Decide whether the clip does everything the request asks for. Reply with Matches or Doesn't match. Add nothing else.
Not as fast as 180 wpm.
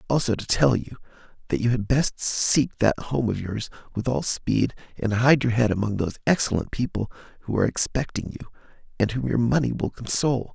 Doesn't match